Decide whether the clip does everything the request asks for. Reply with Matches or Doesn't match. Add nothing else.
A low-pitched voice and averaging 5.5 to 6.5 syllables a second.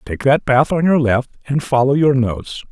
Doesn't match